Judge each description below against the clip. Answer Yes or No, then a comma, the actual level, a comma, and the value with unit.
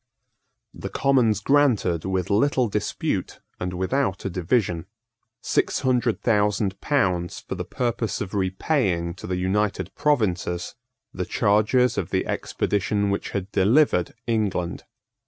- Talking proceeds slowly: Yes, slow, 125 wpm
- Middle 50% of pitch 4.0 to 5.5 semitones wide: Yes, average, 4.7 semitones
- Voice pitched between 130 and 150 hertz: No, low, 100 Hz